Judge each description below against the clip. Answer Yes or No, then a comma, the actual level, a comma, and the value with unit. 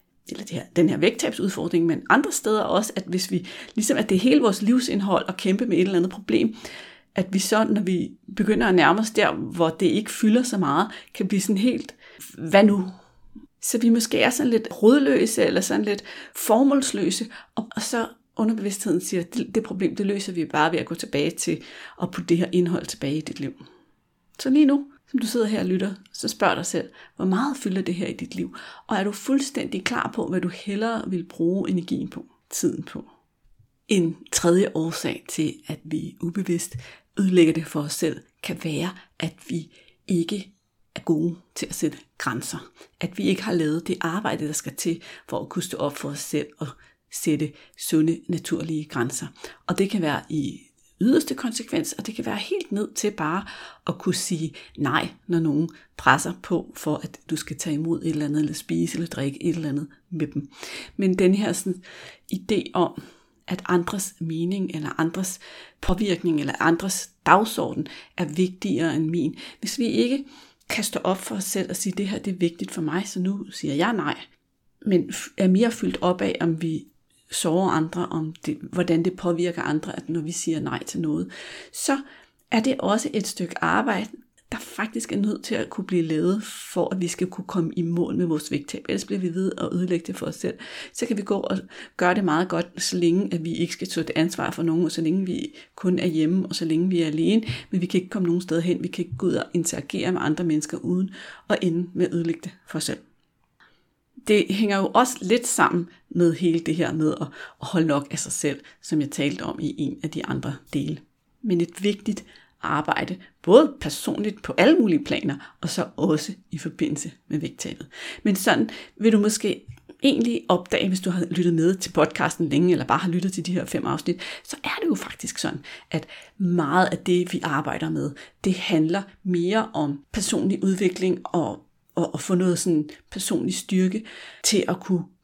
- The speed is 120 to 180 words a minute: No, average, 210 wpm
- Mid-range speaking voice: Yes, medium, 180 Hz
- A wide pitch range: No, average, 3.7 semitones